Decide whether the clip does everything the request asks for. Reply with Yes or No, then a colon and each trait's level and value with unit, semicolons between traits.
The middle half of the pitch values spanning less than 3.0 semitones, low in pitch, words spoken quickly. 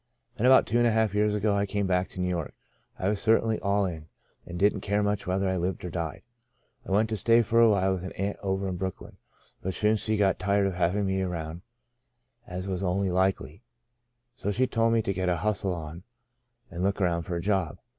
Yes: narrow, 2.5 semitones; very low, 95 Hz; fast, 240 wpm